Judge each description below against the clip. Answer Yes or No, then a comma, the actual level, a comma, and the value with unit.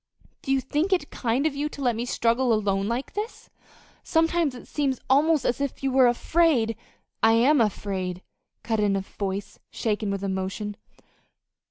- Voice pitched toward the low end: No, high, 240 Hz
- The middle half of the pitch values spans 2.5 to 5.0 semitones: No, wide, 5.4 semitones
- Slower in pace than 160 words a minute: No, average, 180 wpm